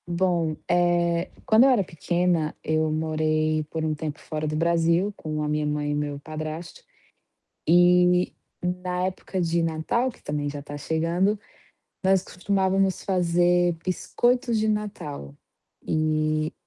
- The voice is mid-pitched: Yes, medium, 170 Hz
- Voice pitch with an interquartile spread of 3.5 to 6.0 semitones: No, average, 2.8 semitones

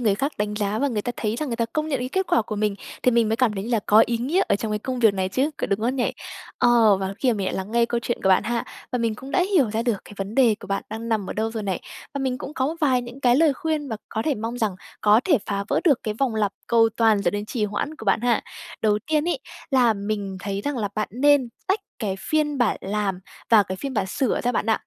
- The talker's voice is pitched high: Yes, high, 230 Hz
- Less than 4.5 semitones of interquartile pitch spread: Yes, average, 3.9 semitones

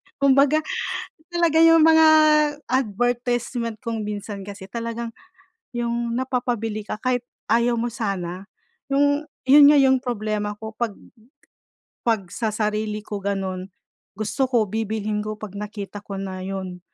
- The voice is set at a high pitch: Yes, high, 220 Hz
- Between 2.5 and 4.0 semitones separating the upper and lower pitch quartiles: Yes, average, 3.2 semitones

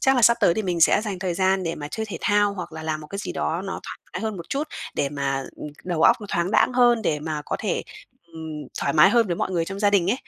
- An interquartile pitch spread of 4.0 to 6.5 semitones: Yes, average, 4.5 semitones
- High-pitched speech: No, medium, 180 Hz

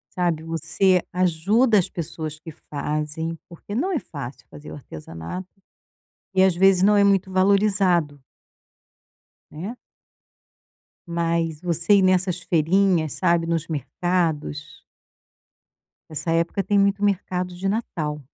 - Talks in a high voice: No, medium, 175 Hz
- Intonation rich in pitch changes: No, average, 3.4 semitones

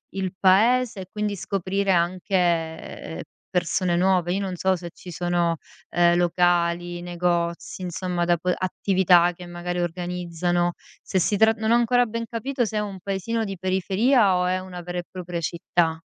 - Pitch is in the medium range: Yes, medium, 180 Hz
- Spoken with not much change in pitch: Yes, narrow, 2.1 semitones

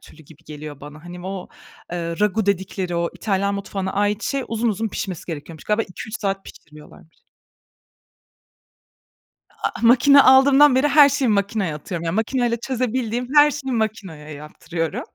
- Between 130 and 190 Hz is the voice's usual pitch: No, high, 200 Hz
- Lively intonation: Yes, wide, 6.0 semitones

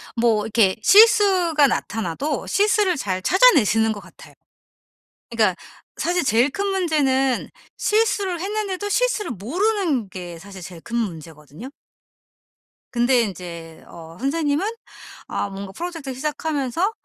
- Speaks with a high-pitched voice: Yes, very high, 265 Hz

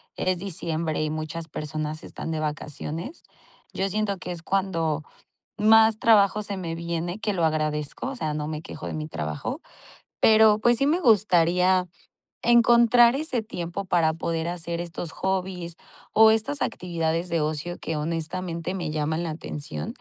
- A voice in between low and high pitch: Yes, medium, 170 Hz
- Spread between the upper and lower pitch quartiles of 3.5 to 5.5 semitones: Yes, average, 4.6 semitones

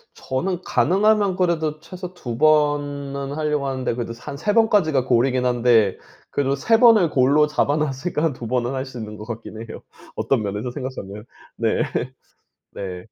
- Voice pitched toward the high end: No, medium, 140 Hz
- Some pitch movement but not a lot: Yes, average, 4.5 semitones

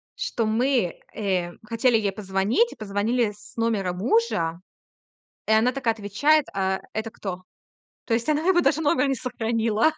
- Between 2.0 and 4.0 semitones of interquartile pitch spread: No, average, 4.4 semitones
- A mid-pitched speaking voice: No, high, 225 Hz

